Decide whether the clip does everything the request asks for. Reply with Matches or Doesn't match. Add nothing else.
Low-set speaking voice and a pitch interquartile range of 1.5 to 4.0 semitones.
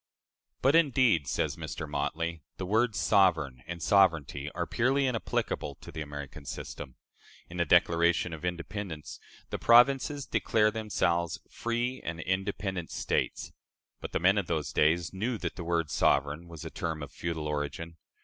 Doesn't match